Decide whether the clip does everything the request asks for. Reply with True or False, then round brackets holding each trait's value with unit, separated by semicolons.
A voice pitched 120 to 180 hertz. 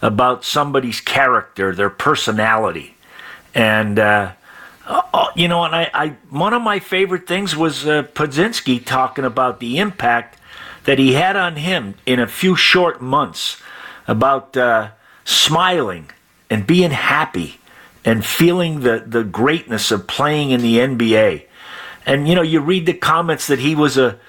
True (135 Hz)